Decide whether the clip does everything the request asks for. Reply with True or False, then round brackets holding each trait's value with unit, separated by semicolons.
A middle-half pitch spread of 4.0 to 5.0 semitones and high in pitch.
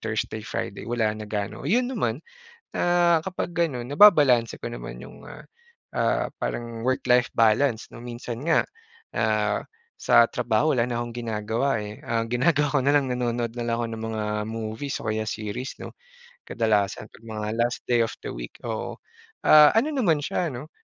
False (4.5 semitones; 120 Hz)